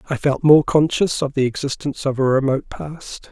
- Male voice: Yes, male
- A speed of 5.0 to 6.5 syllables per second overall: Yes, 5.5 syllables/s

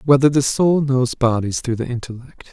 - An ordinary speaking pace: Yes, average, 190 wpm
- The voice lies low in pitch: Yes, low, 130 Hz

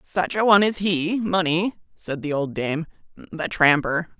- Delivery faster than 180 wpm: No, average, 170 wpm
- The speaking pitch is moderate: Yes, medium, 175 Hz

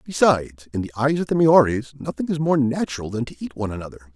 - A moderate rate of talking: No, fast, 230 wpm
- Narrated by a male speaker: Yes, male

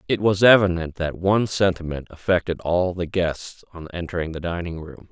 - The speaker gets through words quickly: No, average, 175 wpm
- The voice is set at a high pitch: No, very low, 90 Hz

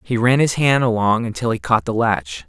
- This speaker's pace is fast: Yes, fast, 240 wpm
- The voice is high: No, low, 115 Hz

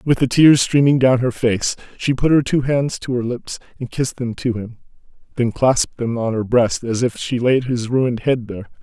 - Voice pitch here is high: No, low, 125 Hz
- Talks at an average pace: No, fast, 230 wpm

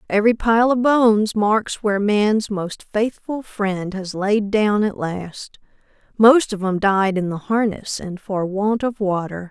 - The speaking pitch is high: Yes, high, 205 Hz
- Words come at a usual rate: Yes, average, 170 wpm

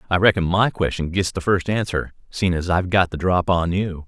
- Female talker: No, male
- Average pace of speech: No, fast, 235 wpm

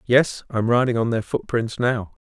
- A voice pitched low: Yes, low, 115 Hz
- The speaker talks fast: No, average, 185 wpm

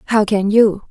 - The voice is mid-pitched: No, high, 210 Hz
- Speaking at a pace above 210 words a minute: No, average, 200 wpm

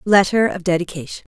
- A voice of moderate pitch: Yes, medium, 180 Hz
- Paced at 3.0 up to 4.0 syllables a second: No, 5.9 syllables/s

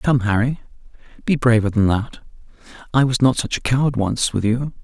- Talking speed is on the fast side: No, average, 185 wpm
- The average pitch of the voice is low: Yes, low, 120 Hz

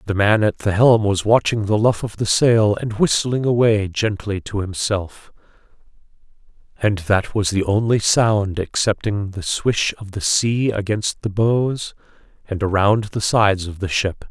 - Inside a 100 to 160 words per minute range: No, average, 170 wpm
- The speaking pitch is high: No, low, 105 Hz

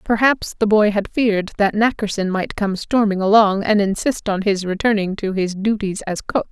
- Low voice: No, high, 205 Hz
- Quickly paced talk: No, average, 195 wpm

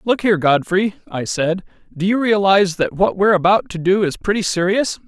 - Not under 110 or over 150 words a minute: No, average, 200 wpm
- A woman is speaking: No, male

